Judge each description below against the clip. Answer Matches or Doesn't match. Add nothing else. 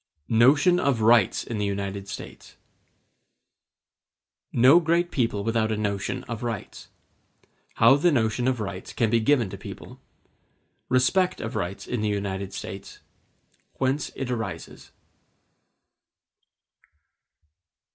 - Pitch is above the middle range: Doesn't match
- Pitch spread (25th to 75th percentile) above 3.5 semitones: Matches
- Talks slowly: Matches